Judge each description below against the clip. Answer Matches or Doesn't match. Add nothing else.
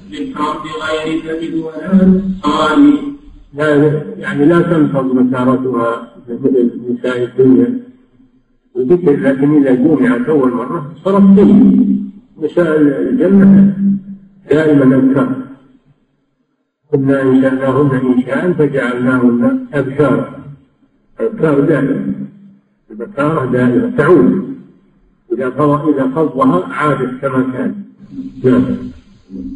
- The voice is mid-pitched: Matches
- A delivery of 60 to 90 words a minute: Matches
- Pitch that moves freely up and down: Matches